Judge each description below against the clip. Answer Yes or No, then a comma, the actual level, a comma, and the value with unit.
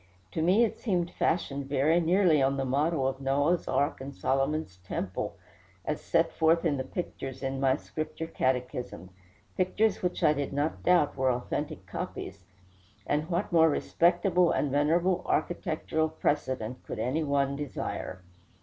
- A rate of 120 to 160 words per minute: Yes, average, 150 wpm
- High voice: No, medium, 150 Hz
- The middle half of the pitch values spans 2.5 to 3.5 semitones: No, average, 3.9 semitones